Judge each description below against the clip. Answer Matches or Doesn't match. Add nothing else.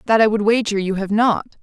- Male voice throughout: Doesn't match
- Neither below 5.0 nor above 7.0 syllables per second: Matches